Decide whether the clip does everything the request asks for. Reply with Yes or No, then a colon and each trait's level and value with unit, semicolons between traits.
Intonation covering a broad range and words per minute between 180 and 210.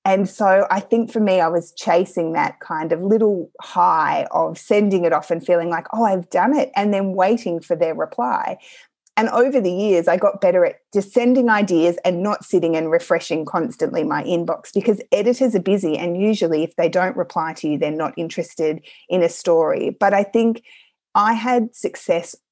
No: average, 4.7 semitones; average, 195 wpm